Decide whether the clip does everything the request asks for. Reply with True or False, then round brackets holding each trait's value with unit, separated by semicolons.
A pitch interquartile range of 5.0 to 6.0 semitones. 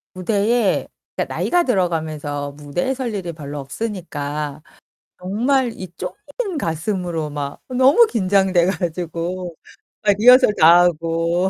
True (5.3 semitones)